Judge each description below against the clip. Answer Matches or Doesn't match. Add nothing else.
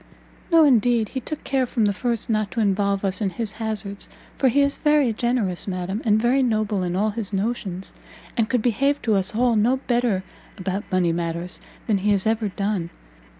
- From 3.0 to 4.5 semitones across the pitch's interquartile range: Matches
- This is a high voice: Matches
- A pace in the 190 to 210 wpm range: Matches